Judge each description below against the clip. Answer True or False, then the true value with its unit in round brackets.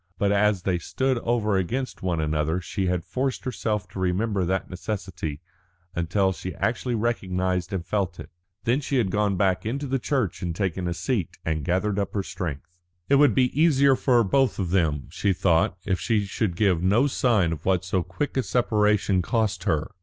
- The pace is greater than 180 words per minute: True (190 wpm)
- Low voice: True (100 Hz)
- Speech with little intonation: False (4.4 semitones)